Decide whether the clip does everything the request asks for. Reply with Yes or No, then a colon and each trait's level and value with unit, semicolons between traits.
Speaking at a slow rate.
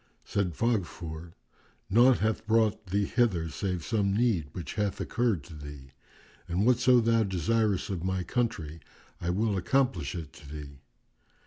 No: average, 145 wpm